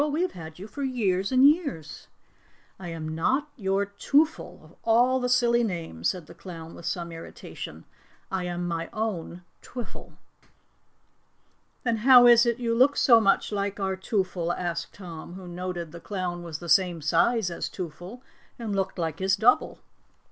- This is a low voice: No, high, 190 Hz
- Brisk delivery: No, average, 170 wpm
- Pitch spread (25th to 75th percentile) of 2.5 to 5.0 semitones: No, wide, 5.6 semitones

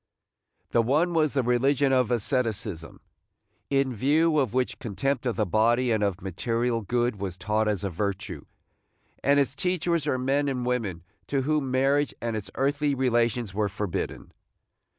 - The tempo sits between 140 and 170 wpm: Yes, average, 160 wpm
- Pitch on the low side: Yes, low, 125 Hz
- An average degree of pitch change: Yes, average, 4.4 semitones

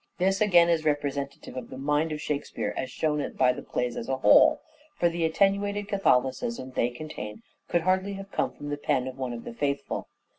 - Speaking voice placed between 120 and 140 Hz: No, medium, 150 Hz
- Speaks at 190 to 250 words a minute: Yes, average, 200 wpm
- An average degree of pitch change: No, wide, 6.0 semitones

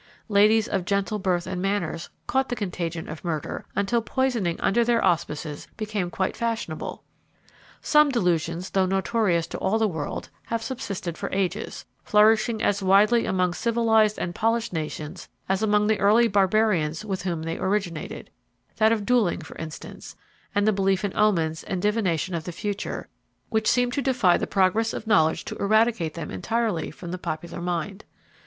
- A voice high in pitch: Yes, high, 195 Hz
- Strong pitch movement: No, average, 4.1 semitones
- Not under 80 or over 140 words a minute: No, average, 165 wpm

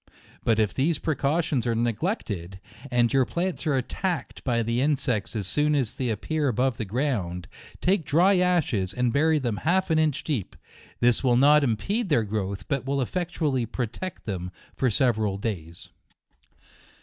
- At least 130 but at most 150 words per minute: No, average, 160 wpm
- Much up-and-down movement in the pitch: Yes, wide, 5.7 semitones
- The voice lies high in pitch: No, low, 130 Hz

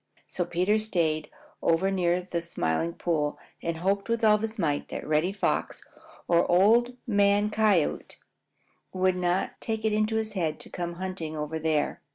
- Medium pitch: Yes, medium, 180 Hz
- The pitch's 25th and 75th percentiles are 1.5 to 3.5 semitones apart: No, average, 4.4 semitones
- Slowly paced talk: No, average, 165 wpm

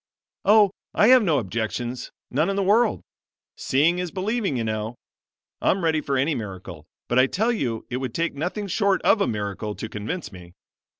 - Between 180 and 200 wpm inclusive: Yes, average, 185 wpm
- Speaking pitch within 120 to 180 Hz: Yes, medium, 140 Hz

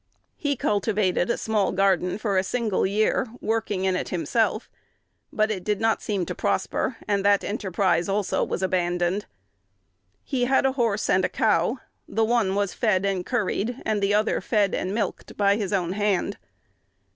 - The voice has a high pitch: Yes, high, 205 Hz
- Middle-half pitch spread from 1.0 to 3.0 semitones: Yes, narrow, 2.6 semitones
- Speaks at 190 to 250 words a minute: No, average, 170 wpm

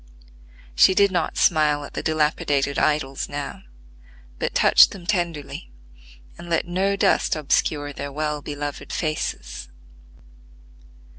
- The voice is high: No, medium, 150 Hz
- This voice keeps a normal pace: No, slow, 120 wpm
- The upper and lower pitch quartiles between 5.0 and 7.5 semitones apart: No, average, 3.2 semitones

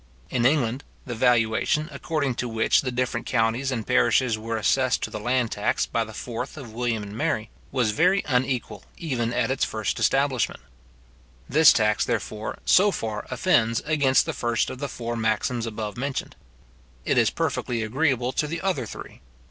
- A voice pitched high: No, low, 125 Hz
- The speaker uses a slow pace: No, average, 170 wpm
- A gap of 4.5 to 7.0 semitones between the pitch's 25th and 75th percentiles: No, average, 3.2 semitones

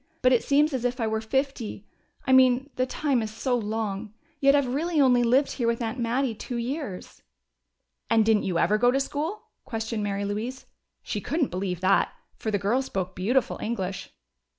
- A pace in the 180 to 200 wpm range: Yes, average, 190 wpm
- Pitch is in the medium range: No, high, 235 Hz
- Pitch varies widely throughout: No, average, 3.9 semitones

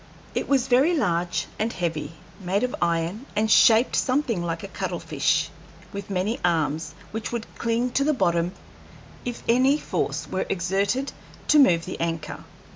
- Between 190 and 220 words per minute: No, average, 155 wpm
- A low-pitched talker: No, high, 200 Hz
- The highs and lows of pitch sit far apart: Yes, wide, 6.3 semitones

